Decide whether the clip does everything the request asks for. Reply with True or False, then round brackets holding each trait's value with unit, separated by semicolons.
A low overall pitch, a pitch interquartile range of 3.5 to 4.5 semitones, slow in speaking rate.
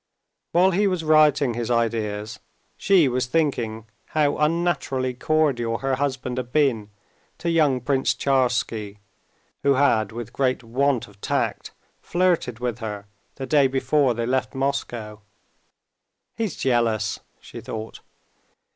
True (130 Hz; 4.1 semitones; 130 wpm)